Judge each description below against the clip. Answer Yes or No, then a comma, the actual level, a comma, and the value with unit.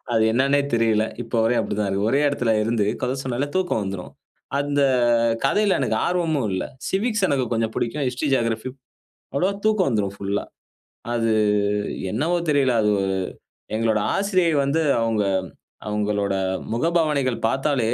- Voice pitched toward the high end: No, low, 125 Hz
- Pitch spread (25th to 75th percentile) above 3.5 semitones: Yes, average, 5.3 semitones